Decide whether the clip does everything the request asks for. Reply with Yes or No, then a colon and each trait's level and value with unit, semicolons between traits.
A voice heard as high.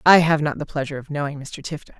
No: medium, 150 Hz